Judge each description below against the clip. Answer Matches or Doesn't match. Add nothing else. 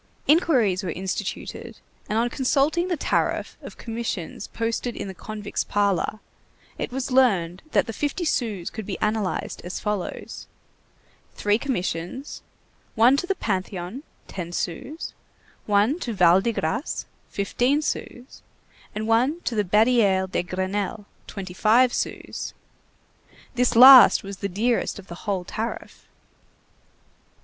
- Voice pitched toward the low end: Doesn't match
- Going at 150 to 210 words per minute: Doesn't match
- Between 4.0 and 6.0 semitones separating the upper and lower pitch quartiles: Matches